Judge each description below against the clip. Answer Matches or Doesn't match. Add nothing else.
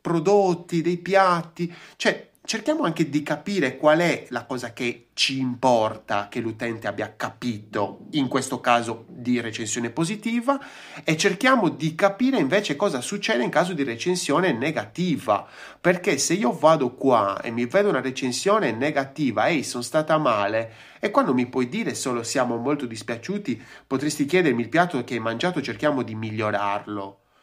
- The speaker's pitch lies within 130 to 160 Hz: Matches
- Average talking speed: Matches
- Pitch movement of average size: Doesn't match